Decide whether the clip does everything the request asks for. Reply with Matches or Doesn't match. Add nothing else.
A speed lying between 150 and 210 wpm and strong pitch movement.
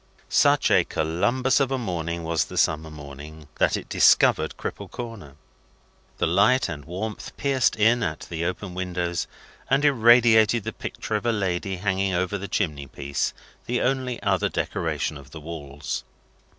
Matches